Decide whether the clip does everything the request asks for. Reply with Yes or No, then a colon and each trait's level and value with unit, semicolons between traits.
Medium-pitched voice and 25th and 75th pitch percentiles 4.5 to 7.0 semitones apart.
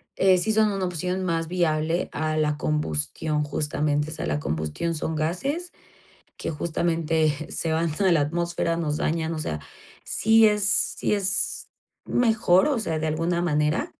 No: medium, 165 Hz; average, 3.2 semitones